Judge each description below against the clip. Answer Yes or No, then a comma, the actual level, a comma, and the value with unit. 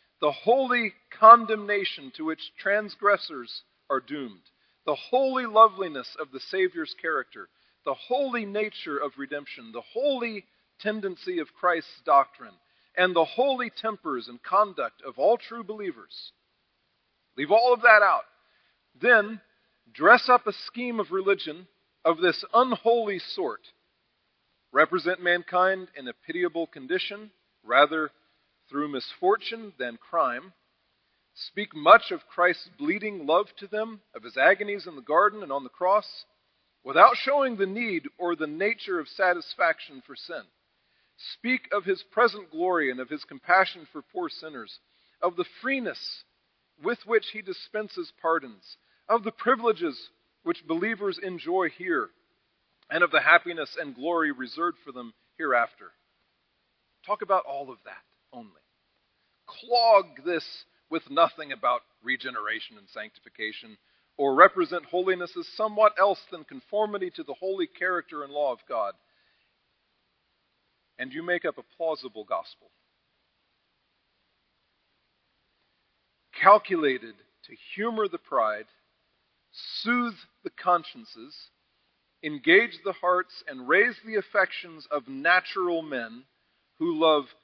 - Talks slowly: Yes, slow, 125 wpm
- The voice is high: Yes, high, 200 Hz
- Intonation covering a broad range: Yes, wide, 6.0 semitones